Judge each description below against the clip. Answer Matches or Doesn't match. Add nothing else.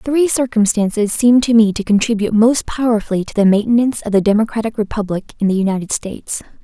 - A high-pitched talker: Matches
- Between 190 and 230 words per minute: Doesn't match